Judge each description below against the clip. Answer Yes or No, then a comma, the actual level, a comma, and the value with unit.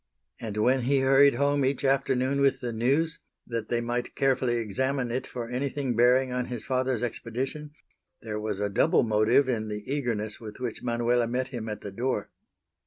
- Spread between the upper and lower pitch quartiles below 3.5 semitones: Yes, narrow, 2.6 semitones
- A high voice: No, low, 125 Hz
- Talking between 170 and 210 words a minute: Yes, average, 180 wpm